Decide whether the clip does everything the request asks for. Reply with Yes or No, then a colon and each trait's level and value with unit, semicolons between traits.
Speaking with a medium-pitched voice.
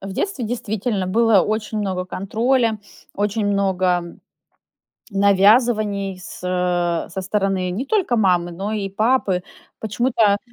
No: high, 200 Hz